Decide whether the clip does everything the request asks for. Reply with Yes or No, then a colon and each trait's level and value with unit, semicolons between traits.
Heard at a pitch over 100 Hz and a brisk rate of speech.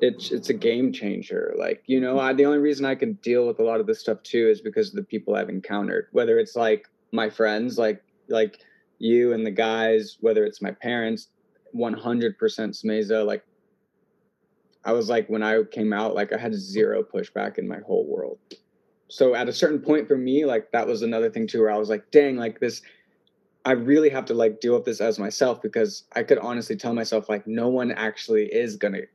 Yes: low, 135 Hz; fast, 220 wpm